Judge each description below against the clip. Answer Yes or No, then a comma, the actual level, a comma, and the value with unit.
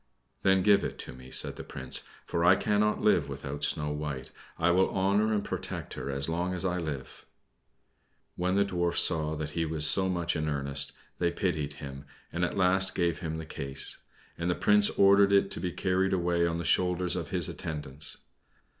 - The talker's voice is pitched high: No, very low, 85 Hz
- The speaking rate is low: No, average, 200 wpm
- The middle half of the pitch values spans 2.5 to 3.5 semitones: No, average, 3.9 semitones